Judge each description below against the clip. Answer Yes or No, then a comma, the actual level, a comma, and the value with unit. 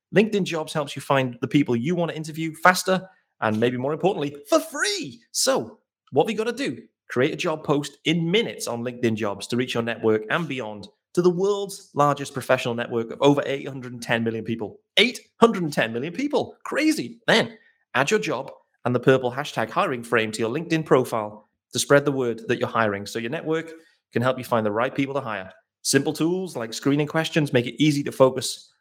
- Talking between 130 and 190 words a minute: No, fast, 205 wpm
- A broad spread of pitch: Yes, wide, 5.7 semitones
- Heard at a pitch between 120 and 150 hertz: Yes, medium, 140 Hz